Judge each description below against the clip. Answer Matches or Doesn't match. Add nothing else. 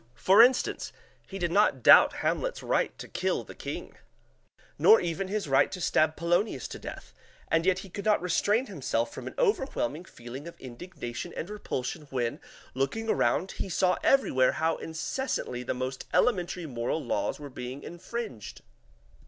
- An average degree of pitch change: Doesn't match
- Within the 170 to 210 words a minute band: Doesn't match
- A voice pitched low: Doesn't match